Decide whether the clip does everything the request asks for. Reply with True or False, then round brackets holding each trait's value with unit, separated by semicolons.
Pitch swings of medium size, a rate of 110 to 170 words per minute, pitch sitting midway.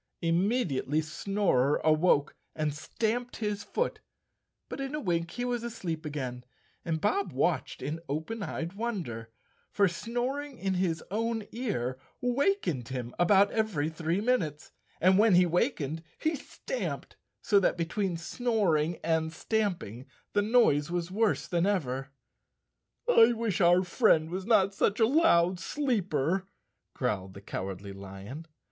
False (6.4 semitones; 140 wpm; 180 Hz)